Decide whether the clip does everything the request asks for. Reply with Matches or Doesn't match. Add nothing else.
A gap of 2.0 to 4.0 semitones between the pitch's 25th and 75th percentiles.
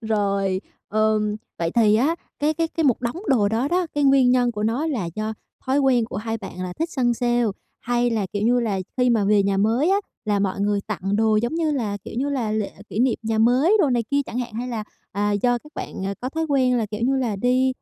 Matches